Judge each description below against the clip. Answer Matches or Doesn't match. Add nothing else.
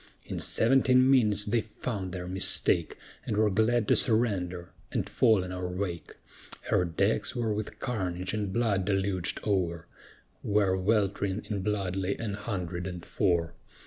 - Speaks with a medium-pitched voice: Doesn't match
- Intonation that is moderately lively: Matches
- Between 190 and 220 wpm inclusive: Doesn't match